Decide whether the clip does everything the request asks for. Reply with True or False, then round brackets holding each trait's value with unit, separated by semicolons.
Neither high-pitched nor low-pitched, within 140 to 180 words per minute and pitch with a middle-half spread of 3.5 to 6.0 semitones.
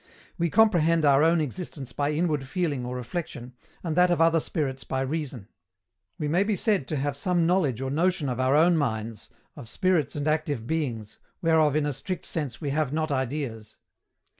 False (150 Hz; 190 wpm; 4.0 semitones)